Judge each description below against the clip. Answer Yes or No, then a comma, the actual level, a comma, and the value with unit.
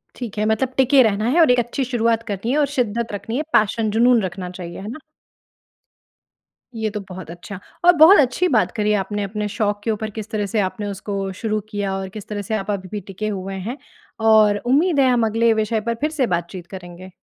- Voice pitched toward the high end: Yes, high, 215 Hz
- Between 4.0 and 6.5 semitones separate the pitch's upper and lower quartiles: No, average, 3.0 semitones